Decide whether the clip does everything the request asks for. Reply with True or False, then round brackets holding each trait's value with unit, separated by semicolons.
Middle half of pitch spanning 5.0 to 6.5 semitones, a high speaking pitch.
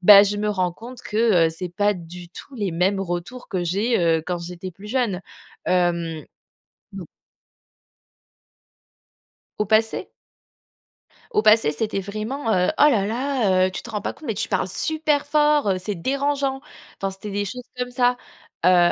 True (5.3 semitones; 205 Hz)